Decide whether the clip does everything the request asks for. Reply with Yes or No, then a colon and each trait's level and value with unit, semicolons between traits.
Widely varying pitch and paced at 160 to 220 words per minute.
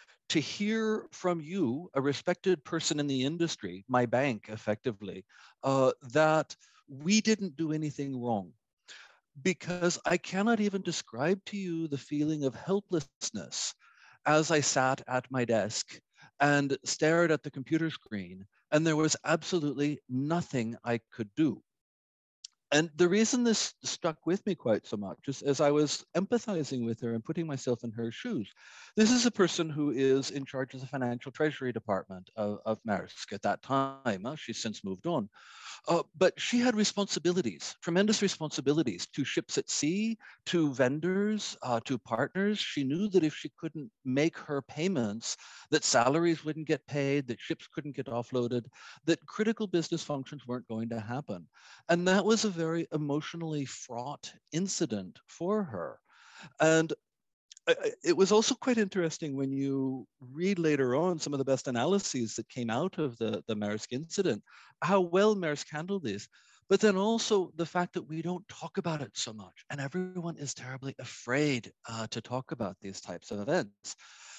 Yes: wide, 5.8 semitones; average, 165 wpm